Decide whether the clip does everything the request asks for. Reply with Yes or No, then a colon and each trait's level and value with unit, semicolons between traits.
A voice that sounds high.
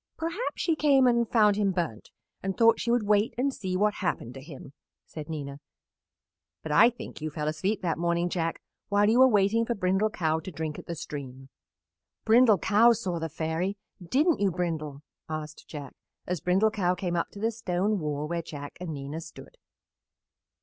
No: medium, 180 Hz